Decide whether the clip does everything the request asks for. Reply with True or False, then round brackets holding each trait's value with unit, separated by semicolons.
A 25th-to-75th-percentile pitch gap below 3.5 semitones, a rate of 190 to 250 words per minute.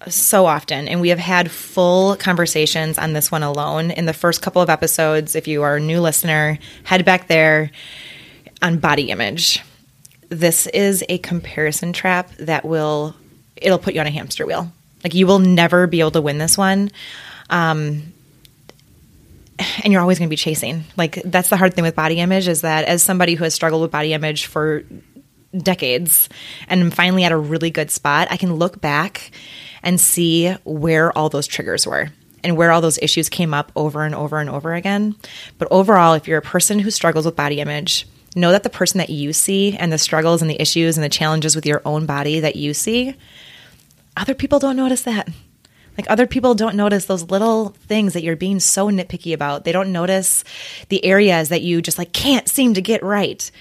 True (3.1 semitones; 200 wpm)